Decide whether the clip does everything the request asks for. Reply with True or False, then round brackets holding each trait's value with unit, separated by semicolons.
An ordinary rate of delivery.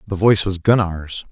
True (180 wpm)